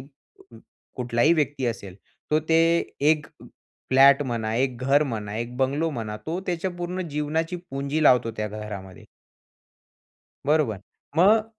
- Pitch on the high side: No, medium, 140 Hz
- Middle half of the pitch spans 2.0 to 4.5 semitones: No, wide, 5.6 semitones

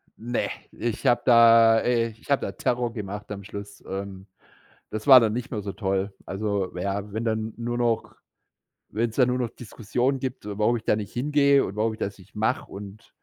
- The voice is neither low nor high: No, low, 110 Hz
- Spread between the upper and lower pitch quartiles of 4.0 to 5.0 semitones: No, average, 2.8 semitones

